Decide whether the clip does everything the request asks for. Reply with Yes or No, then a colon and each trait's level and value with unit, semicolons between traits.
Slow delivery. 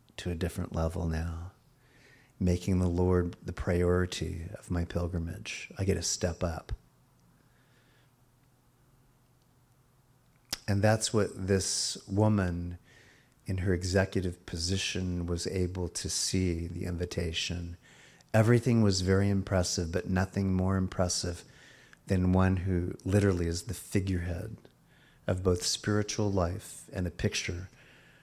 Yes: slow, 115 wpm